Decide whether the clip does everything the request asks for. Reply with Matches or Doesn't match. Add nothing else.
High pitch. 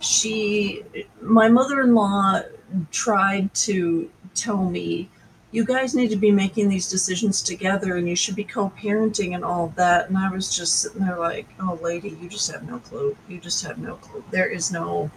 Matches